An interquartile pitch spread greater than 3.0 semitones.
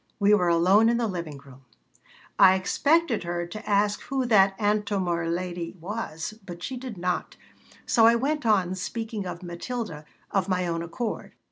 Yes: average, 4.4 semitones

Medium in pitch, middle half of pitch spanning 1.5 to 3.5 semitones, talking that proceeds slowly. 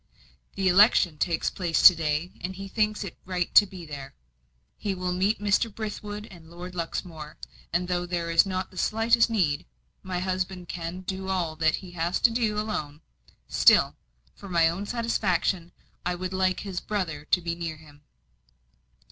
No: medium, 180 Hz; average, 2.8 semitones; average, 175 wpm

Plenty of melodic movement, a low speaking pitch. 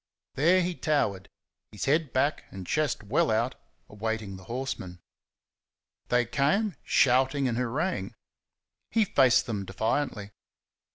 Yes: wide, 5.8 semitones; low, 125 Hz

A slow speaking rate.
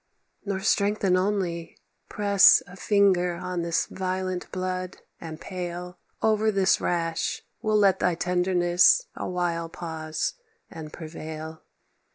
Yes: slow, 120 wpm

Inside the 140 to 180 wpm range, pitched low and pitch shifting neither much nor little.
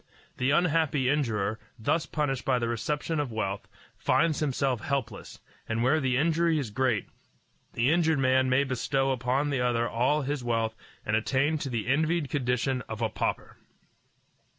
Yes: average, 160 wpm; low, 130 Hz; average, 3.8 semitones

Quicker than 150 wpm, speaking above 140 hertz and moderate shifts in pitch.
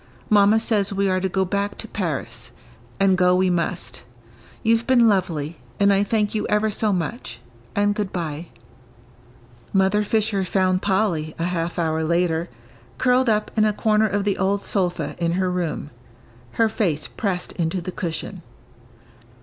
Yes: average, 160 wpm; high, 190 Hz; average, 3.3 semitones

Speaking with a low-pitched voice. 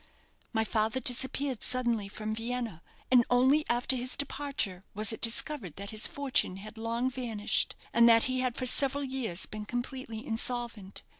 No: high, 240 Hz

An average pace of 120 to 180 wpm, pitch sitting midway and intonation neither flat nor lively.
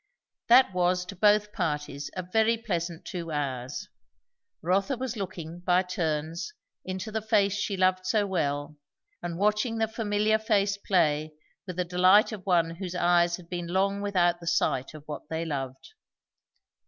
Yes: average, 160 wpm; medium, 180 Hz; average, 3.6 semitones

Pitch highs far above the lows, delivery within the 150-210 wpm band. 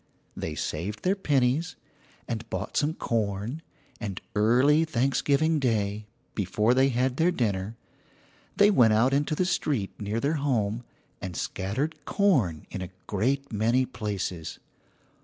No: wide, 5.8 semitones; slow, 135 wpm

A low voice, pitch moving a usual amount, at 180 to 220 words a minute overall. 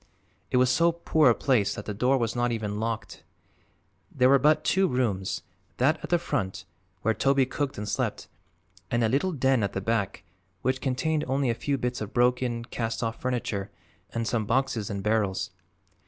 Yes: low, 120 Hz; average, 3.5 semitones; average, 185 wpm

